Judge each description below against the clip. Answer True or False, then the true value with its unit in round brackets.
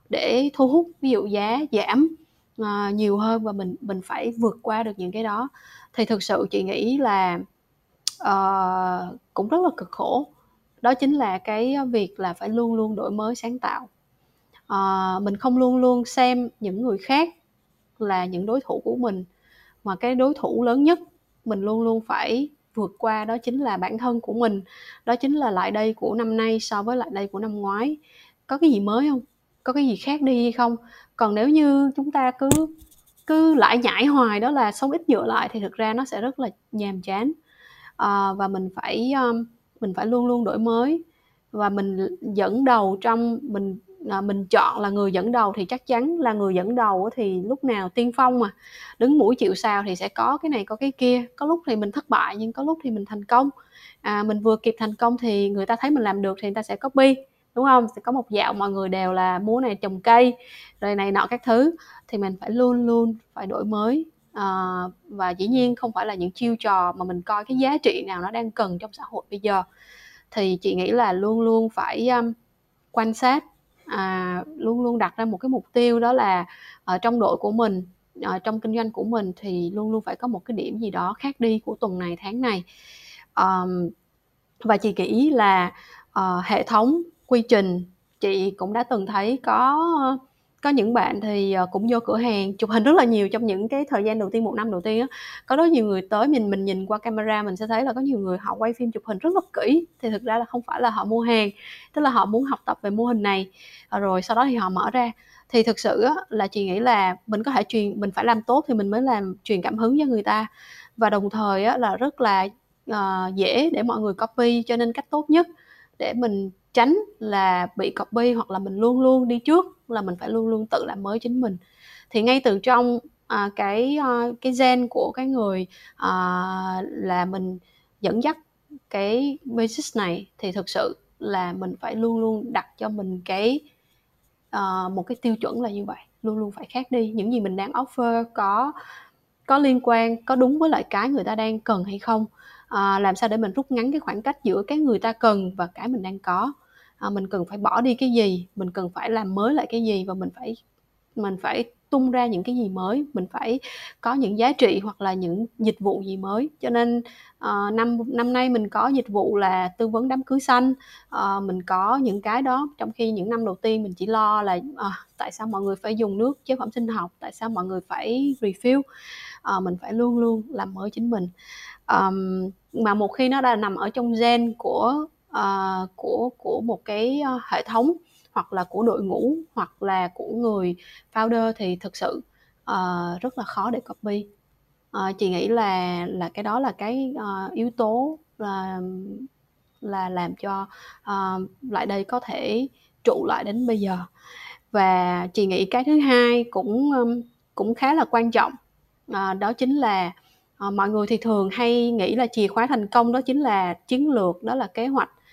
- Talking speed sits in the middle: True (220 wpm)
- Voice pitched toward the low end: False (225 Hz)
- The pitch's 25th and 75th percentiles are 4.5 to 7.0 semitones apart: False (4.0 semitones)